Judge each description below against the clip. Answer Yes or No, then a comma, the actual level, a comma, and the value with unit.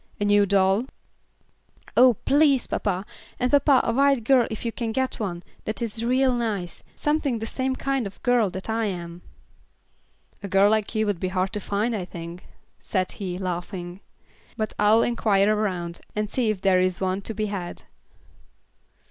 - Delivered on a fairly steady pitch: No, average, 4.0 semitones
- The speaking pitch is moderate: No, high, 210 Hz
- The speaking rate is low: No, average, 175 wpm